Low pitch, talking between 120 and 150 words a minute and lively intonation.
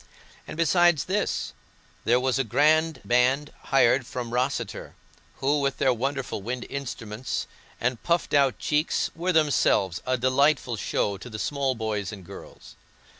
No: low, 130 Hz; average, 145 wpm; average, 3.7 semitones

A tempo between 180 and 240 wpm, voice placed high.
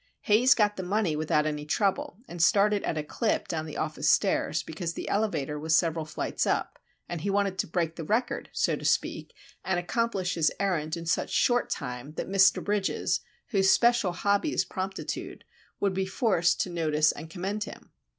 No: average, 190 wpm; medium, 180 Hz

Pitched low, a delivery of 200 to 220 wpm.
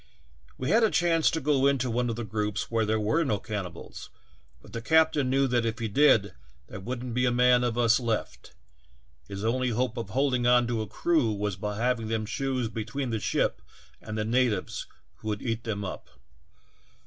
Yes: low, 120 Hz; fast, 205 wpm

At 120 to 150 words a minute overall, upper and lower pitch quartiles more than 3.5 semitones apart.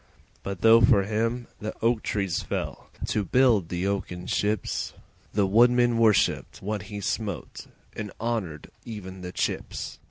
No: average, 145 wpm; average, 3.1 semitones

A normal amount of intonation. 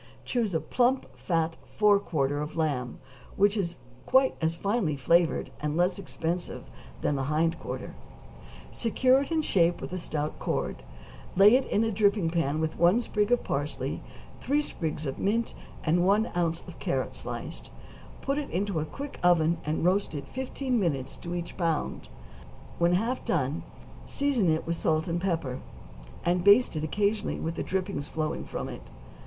Yes: average, 4.8 semitones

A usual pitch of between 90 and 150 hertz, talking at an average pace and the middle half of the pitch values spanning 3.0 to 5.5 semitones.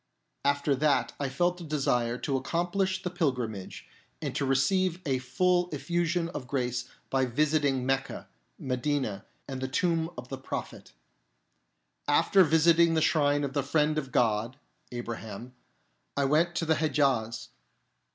Yes: medium, 140 Hz; average, 150 wpm; average, 4.3 semitones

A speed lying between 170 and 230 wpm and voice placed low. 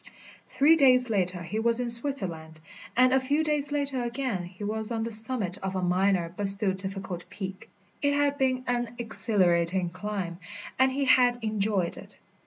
No: average, 175 wpm; high, 220 Hz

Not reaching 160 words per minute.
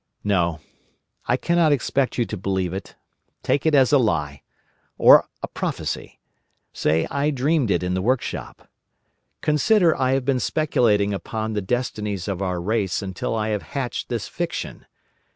Yes: average, 150 wpm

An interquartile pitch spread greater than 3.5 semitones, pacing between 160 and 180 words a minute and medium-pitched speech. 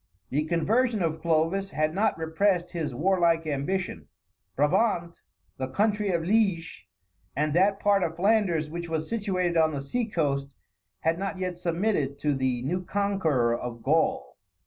No: average, 4.4 semitones; average, 150 wpm; medium, 170 Hz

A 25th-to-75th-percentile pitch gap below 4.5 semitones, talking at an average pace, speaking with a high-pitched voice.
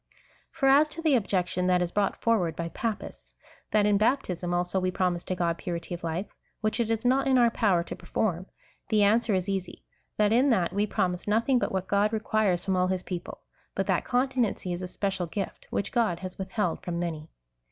No: average, 3.9 semitones; fast, 215 wpm; high, 195 Hz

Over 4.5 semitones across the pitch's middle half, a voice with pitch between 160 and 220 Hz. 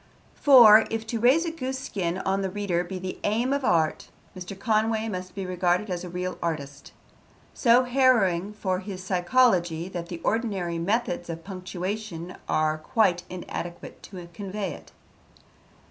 No: average, 4.0 semitones; high, 190 Hz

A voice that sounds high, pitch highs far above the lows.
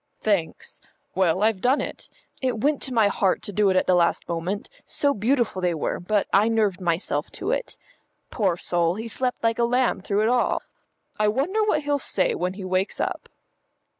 No: high, 210 Hz; average, 4.9 semitones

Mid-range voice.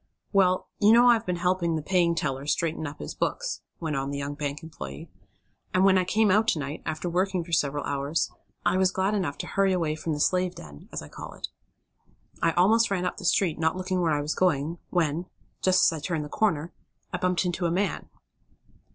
Yes: medium, 175 Hz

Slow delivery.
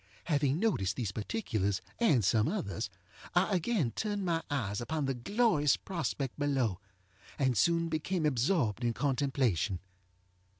Yes: slow, 130 wpm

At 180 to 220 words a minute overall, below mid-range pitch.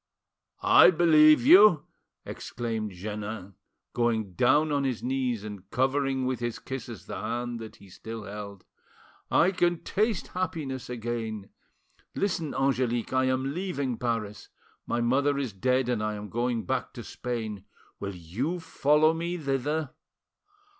No: slow, 135 wpm; low, 125 Hz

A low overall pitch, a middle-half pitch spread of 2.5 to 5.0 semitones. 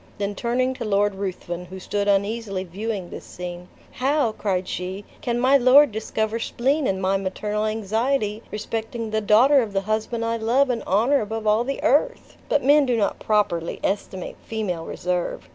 No: high, 215 Hz; average, 3.5 semitones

